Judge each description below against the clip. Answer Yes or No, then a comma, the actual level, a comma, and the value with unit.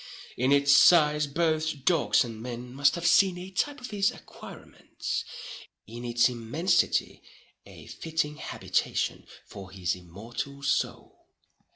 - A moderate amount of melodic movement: No, wide, 5.8 semitones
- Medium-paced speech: No, slow, 125 wpm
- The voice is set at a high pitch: No, medium, 140 Hz